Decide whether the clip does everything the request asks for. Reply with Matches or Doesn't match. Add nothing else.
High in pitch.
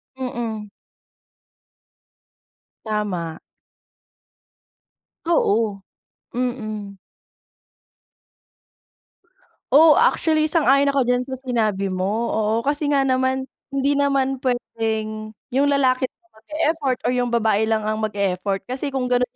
Matches